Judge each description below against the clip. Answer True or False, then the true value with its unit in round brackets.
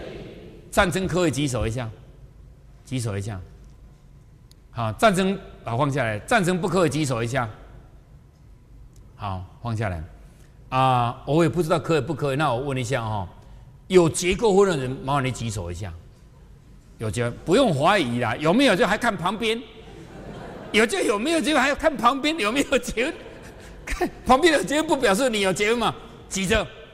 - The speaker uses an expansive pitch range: True (8.4 semitones)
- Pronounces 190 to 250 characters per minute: True (245 characters per minute)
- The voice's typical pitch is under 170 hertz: True (140 Hz)